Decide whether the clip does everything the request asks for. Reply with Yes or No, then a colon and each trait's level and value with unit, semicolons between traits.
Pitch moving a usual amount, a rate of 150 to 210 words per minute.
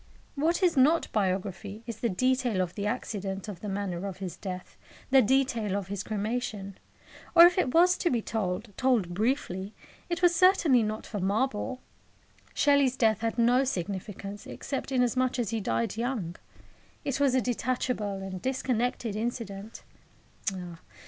Yes: average, 4.7 semitones; average, 155 wpm